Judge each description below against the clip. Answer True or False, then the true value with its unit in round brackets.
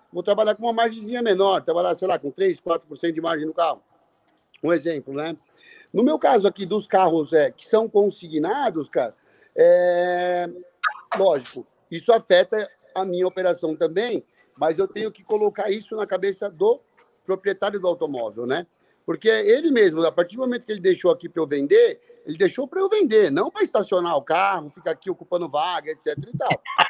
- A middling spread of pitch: False (6.2 semitones)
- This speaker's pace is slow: False (185 wpm)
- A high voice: True (195 Hz)